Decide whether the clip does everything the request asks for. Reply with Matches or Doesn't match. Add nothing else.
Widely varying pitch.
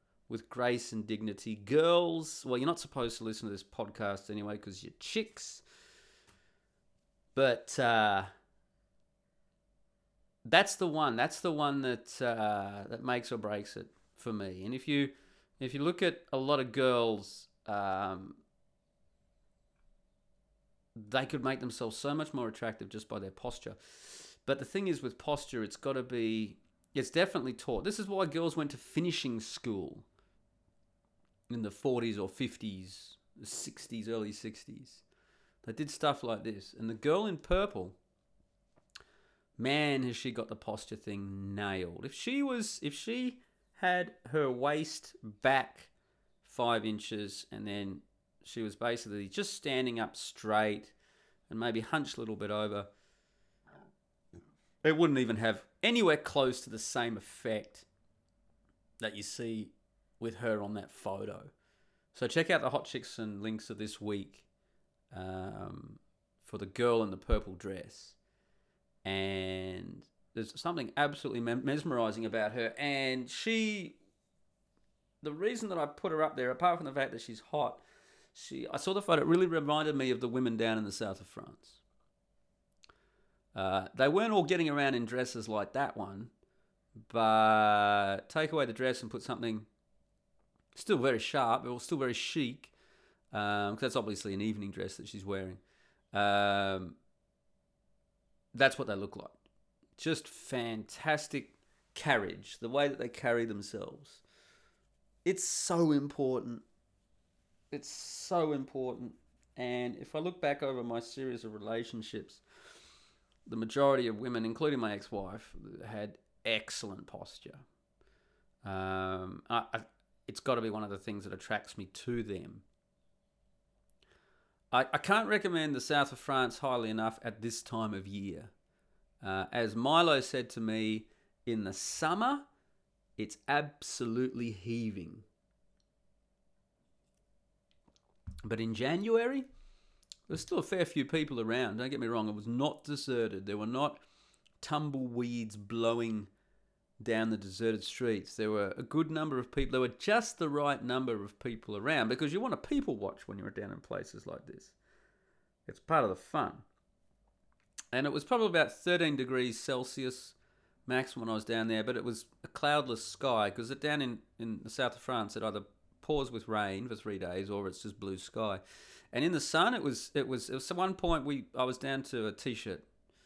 Doesn't match